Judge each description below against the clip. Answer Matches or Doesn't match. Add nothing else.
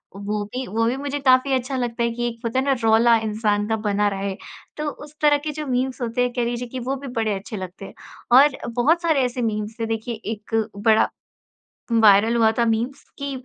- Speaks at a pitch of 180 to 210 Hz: Doesn't match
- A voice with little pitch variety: Doesn't match